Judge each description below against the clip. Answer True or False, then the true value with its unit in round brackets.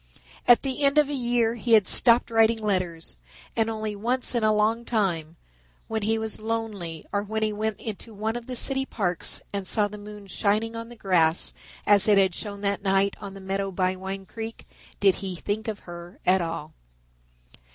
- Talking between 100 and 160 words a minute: False (200 wpm)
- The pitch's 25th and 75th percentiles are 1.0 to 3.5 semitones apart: True (2.7 semitones)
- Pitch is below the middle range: False (210 Hz)